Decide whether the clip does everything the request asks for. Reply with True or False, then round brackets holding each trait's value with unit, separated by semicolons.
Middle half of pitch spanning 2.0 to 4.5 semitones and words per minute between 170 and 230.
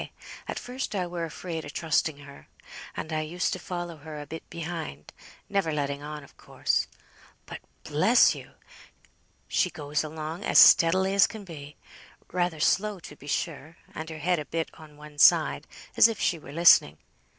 True (2.8 semitones; 175 wpm)